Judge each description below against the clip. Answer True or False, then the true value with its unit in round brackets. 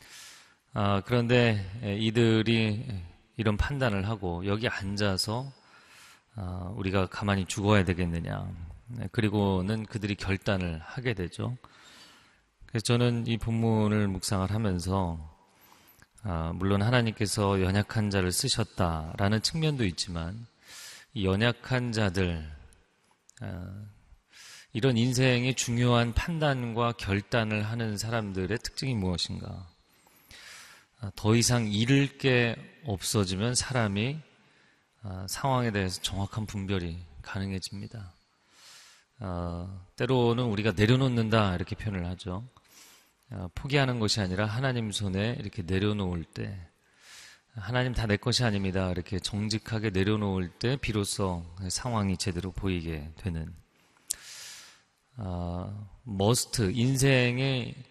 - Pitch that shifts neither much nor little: True (3.7 semitones)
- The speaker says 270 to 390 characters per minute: False (250 characters per minute)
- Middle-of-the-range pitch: False (105 Hz)